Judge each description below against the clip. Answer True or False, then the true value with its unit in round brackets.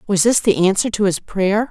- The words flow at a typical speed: False (245 wpm)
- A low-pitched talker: False (200 Hz)